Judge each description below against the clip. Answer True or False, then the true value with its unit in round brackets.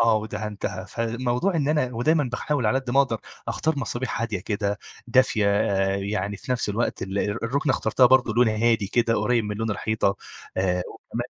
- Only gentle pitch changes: False (3.5 semitones)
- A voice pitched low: True (115 Hz)